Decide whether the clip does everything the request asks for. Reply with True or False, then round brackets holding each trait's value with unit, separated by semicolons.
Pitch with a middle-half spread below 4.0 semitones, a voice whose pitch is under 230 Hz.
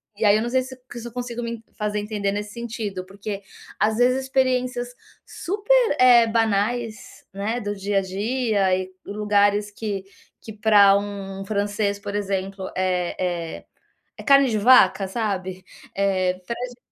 True (3.3 semitones; 210 Hz)